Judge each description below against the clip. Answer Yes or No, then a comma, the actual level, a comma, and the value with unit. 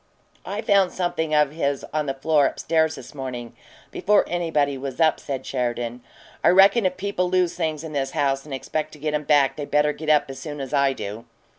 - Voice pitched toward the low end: No, medium, 150 Hz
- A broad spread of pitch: No, average, 3.4 semitones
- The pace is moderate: No, fast, 220 wpm